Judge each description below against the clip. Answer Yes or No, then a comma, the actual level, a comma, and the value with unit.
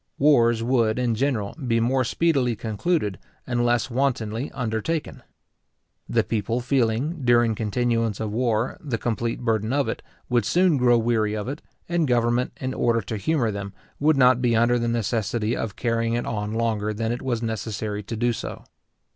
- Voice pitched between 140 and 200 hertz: No, low, 120 Hz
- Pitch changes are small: Yes, narrow, 2.3 semitones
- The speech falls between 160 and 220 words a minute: Yes, average, 170 wpm